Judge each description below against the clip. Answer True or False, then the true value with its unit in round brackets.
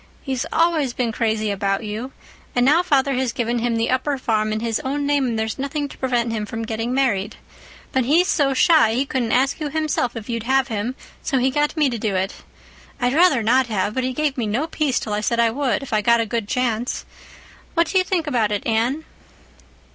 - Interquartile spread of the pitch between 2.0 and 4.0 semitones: True (3.7 semitones)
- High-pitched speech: True (250 Hz)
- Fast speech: True (225 wpm)